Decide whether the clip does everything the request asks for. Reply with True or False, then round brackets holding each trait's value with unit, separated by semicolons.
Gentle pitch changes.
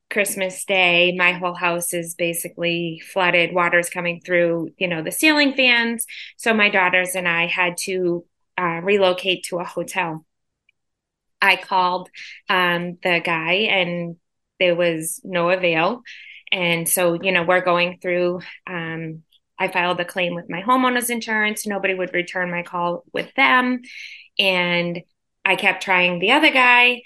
True (1.8 semitones)